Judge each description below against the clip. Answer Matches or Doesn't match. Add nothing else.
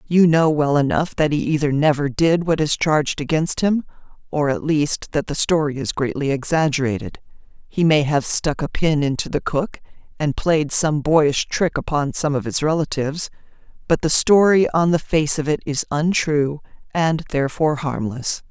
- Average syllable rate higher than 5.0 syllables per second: Doesn't match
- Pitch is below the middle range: Doesn't match